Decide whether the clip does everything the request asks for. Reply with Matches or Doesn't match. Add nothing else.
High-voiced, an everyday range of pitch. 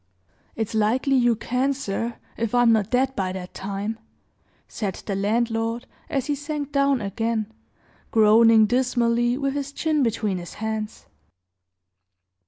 Matches